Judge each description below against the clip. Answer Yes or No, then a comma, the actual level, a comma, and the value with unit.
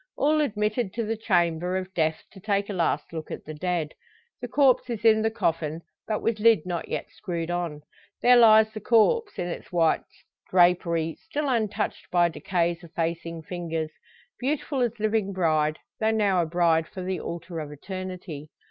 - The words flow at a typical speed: Yes, average, 175 wpm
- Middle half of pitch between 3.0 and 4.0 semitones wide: No, average, 4.7 semitones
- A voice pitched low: No, medium, 180 Hz